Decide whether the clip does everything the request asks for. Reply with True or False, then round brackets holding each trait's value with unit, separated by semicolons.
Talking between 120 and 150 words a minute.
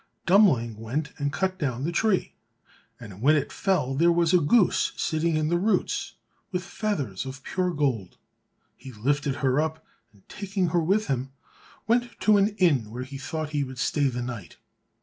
False (180 wpm)